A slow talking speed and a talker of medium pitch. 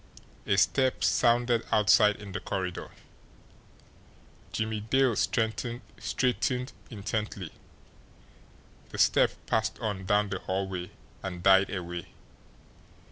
No: slow, 95 wpm; low, 105 Hz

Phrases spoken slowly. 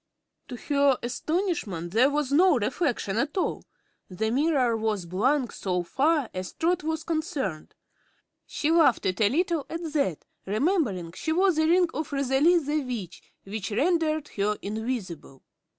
No: average, 145 wpm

